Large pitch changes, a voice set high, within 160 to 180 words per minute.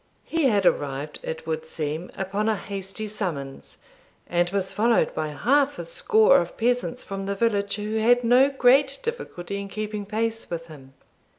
Yes: wide, 5.8 semitones; high, 205 Hz; average, 170 wpm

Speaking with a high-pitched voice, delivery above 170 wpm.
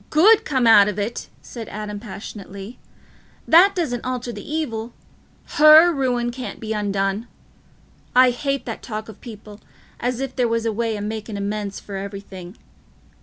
No: high, 225 Hz; average, 160 wpm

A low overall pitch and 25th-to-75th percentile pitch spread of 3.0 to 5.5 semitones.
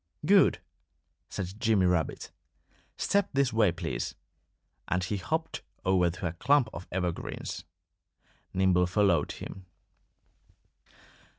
Yes: very low, 95 Hz; average, 4.1 semitones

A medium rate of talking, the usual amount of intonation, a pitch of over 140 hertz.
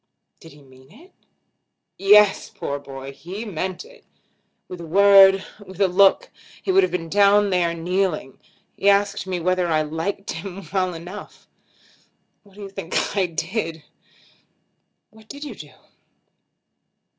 Yes: average, 145 wpm; average, 3.5 semitones; high, 190 Hz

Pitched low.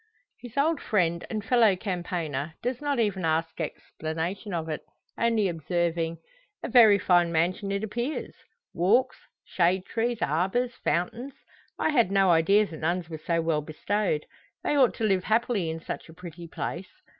No: medium, 185 Hz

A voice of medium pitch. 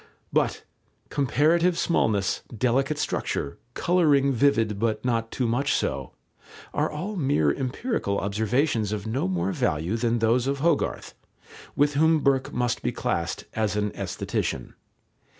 No: low, 125 Hz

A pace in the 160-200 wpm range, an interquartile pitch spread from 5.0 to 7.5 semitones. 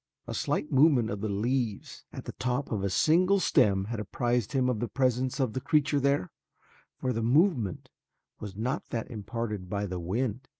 No: average, 185 wpm; average, 4.2 semitones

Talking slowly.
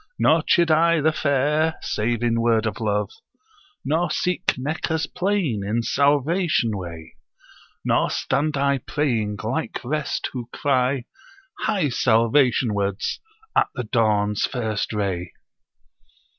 Yes: slow, 120 wpm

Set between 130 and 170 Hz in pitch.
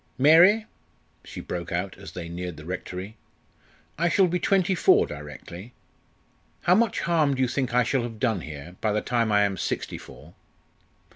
No: low, 115 Hz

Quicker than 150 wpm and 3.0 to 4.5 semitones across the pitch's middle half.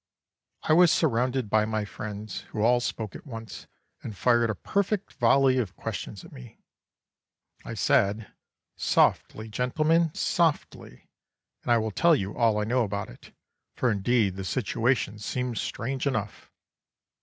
No: average, 145 wpm; average, 3.6 semitones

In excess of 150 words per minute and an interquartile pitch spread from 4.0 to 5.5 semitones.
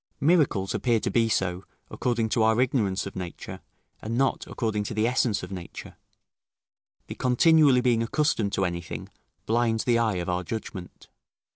Yes: average, 160 wpm; average, 4.3 semitones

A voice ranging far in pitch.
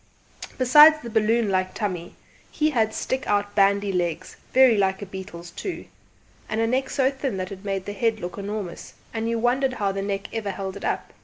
No: average, 3.6 semitones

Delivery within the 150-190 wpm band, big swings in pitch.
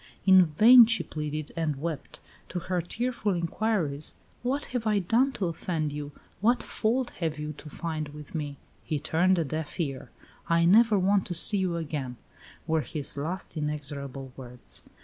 No: average, 170 wpm; average, 5.0 semitones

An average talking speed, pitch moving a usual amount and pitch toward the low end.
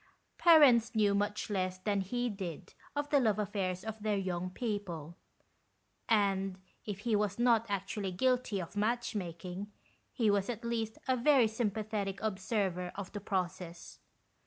No: average, 150 wpm; average, 3.2 semitones; high, 205 Hz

